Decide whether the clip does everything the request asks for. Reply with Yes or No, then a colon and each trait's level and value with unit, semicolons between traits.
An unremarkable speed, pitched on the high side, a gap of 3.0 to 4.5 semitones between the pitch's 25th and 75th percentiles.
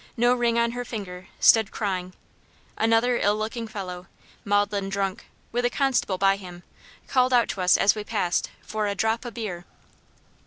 Yes: average, 170 wpm; high, 210 Hz; average, 3.3 semitones